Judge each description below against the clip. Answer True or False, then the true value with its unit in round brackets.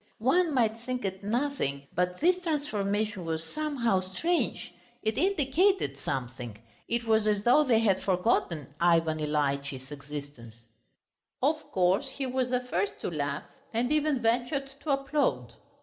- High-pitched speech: True (215 Hz)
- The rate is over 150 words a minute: False (140 wpm)